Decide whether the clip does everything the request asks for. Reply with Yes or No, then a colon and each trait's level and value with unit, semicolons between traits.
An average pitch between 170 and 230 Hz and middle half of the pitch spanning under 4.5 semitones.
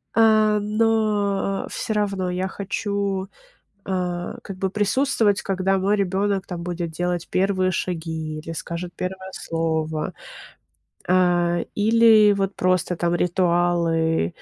Yes: medium, 185 Hz; narrow, 2.6 semitones